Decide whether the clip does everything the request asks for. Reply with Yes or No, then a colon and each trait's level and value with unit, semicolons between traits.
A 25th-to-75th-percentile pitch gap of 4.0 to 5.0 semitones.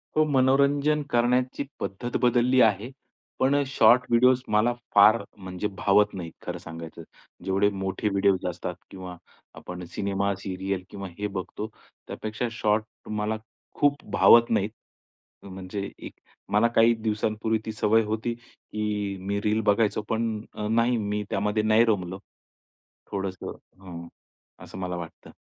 No: average, 3.1 semitones